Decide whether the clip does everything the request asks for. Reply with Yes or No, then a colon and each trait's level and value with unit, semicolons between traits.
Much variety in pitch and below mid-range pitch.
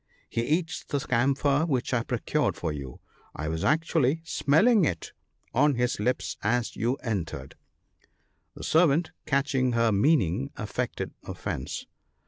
Yes: wide, 6.1 semitones; low, 130 Hz